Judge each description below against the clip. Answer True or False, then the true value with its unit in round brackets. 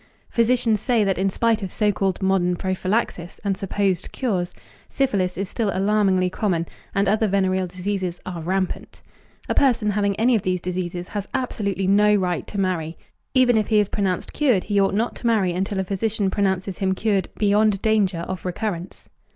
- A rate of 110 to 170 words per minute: False (180 wpm)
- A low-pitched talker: False (195 Hz)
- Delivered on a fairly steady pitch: True (2.3 semitones)